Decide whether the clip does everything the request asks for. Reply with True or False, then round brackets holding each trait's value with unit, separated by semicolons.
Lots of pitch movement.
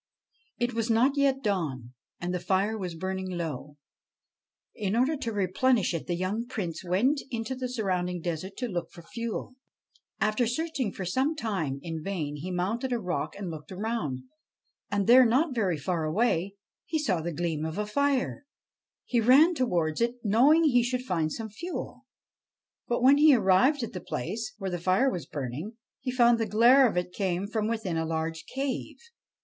True (6.0 semitones)